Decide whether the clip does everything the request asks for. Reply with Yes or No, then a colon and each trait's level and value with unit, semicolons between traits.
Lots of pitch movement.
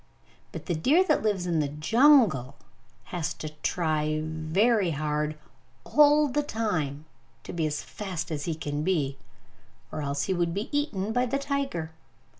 Yes: wide, 6.9 semitones